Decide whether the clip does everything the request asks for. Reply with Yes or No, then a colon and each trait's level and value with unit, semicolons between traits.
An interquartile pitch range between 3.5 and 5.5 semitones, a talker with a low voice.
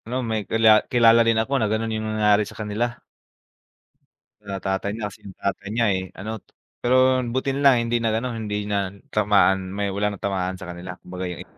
No: average, 2.7 semitones; low, 105 Hz